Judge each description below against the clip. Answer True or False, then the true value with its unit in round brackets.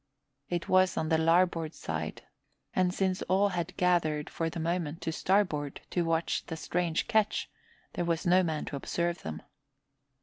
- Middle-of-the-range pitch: True (170 Hz)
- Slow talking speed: False (165 wpm)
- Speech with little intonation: True (2.2 semitones)